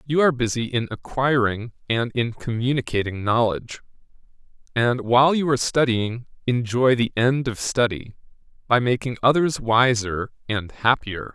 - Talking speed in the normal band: No, slow, 130 wpm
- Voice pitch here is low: Yes, low, 120 Hz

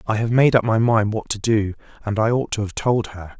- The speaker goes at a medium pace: No, fast, 285 wpm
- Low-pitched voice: Yes, low, 110 Hz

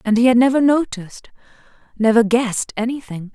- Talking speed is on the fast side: No, average, 145 wpm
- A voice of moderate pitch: No, high, 235 Hz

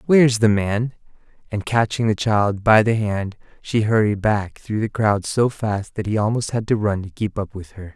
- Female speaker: No, male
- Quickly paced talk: Yes, fast, 225 wpm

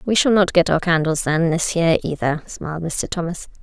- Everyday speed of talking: No, fast, 215 wpm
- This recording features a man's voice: No, female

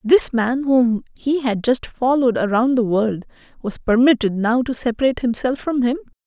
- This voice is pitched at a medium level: No, high, 245 Hz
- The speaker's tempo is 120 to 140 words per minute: No, average, 170 wpm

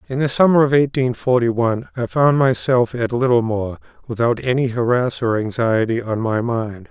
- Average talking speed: Yes, average, 175 wpm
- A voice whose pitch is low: Yes, low, 120 Hz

